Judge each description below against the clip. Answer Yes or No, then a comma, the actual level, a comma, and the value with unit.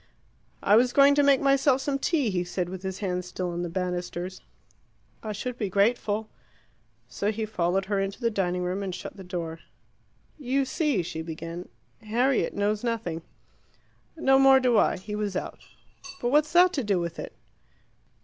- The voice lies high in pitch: Yes, high, 205 Hz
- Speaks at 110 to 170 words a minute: No, average, 180 wpm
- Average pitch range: No, wide, 5.9 semitones